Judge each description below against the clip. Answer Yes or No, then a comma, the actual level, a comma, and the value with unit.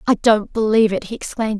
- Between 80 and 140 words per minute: No, fast, 225 wpm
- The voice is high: Yes, high, 215 Hz